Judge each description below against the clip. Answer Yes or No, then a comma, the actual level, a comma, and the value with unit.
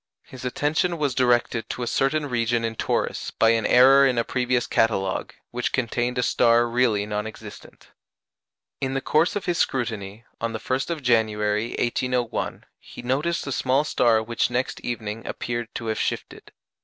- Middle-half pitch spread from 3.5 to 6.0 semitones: No, narrow, 2.6 semitones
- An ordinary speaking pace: Yes, average, 170 wpm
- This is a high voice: No, low, 120 Hz